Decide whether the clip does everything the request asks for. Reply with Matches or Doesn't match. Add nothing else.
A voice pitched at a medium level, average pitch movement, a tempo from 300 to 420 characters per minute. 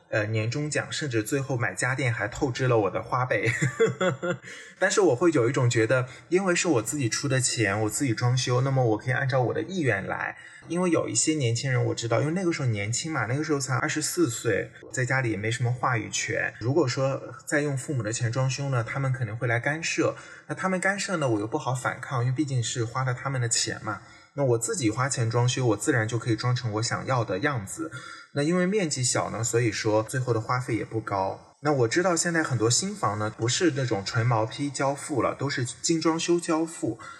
Doesn't match